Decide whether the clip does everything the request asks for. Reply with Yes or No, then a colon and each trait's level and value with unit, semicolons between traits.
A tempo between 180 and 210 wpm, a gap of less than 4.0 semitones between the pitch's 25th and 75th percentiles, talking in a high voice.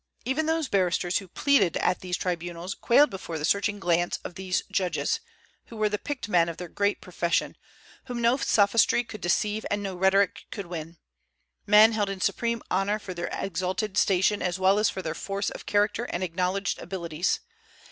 Yes: average, 185 wpm; average, 3.0 semitones; high, 195 Hz